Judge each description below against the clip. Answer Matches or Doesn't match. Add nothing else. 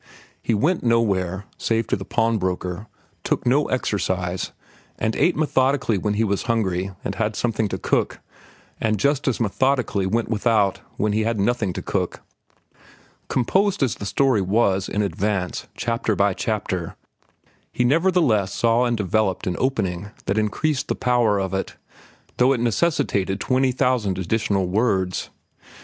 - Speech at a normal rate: Matches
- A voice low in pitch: Matches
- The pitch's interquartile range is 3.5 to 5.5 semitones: Matches